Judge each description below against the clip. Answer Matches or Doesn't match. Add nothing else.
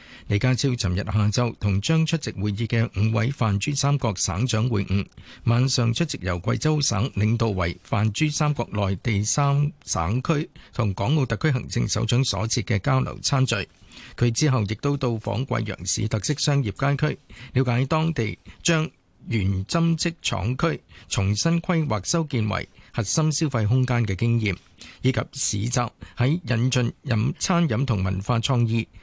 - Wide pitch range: Doesn't match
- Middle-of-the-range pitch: Doesn't match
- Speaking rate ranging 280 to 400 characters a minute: Doesn't match